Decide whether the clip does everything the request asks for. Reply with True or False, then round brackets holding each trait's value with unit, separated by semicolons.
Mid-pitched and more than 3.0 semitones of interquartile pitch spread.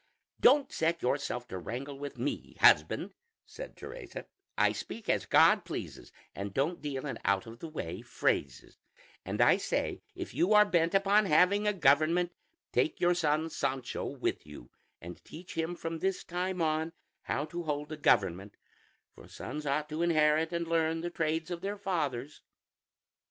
True (160 Hz; 4.0 semitones)